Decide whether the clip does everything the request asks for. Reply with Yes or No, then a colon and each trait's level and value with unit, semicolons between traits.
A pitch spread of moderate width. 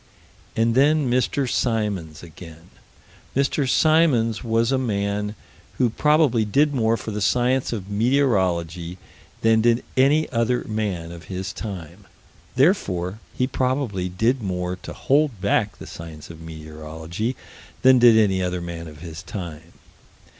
No: wide, 6.2 semitones